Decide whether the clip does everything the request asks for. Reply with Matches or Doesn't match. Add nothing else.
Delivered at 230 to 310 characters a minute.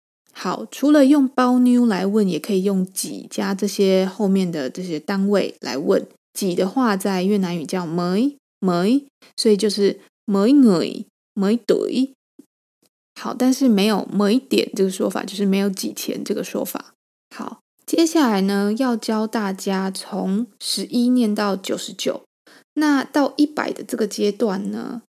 Doesn't match